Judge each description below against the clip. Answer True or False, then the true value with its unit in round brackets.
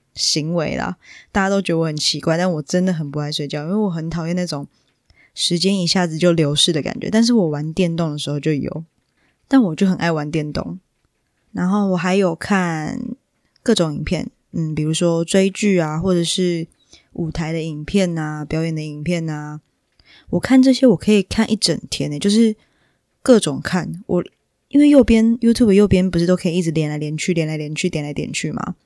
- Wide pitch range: False (4.0 semitones)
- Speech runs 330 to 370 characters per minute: False (300 characters per minute)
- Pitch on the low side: False (170 Hz)